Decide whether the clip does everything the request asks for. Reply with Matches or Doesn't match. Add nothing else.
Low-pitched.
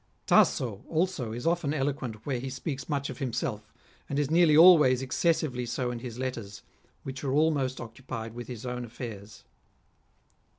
Matches